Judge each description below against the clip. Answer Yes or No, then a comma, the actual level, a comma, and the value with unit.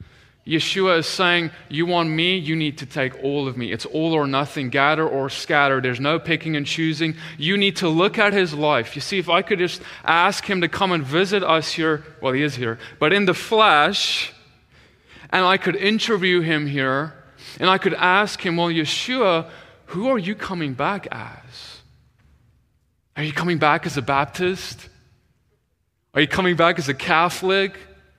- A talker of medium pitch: Yes, medium, 160 Hz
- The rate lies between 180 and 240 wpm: Yes, average, 185 wpm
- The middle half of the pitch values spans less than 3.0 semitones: No, average, 4.3 semitones